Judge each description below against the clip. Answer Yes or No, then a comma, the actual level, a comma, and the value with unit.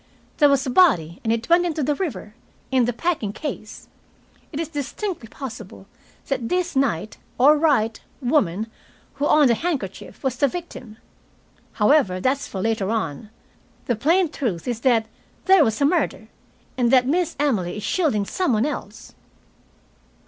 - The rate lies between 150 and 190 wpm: Yes, average, 160 wpm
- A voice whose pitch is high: Yes, very high, 260 Hz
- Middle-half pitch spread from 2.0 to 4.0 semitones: No, wide, 5.5 semitones